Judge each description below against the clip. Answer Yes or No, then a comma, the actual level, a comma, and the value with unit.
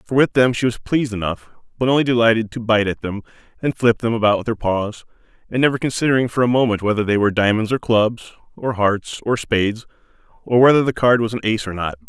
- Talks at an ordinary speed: No, fast, 230 wpm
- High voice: No, low, 115 Hz